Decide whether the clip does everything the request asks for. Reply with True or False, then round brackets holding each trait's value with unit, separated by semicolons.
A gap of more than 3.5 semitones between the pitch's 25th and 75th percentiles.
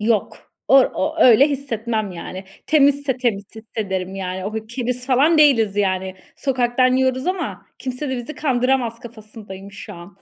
True (4.5 semitones)